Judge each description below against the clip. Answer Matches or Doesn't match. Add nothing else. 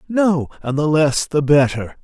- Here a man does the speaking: Matches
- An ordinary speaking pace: Matches